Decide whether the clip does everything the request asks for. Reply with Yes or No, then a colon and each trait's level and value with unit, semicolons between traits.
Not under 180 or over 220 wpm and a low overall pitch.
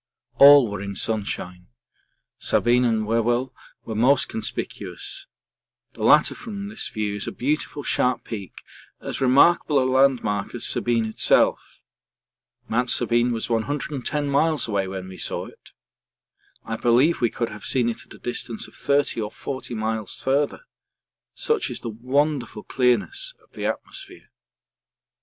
No: average, 145 wpm; low, 125 Hz